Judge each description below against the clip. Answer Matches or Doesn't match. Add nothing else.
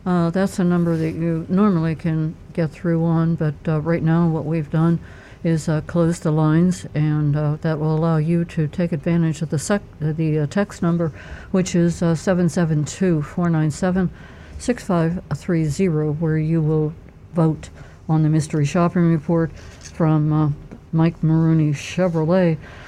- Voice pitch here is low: Doesn't match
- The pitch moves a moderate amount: Doesn't match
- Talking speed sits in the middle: Matches